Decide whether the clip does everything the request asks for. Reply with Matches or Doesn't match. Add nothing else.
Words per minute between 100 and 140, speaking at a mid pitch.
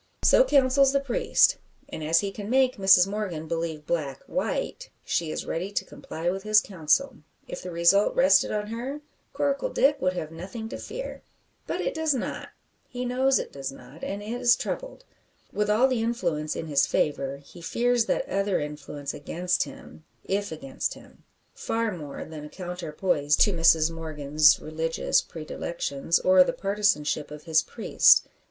Doesn't match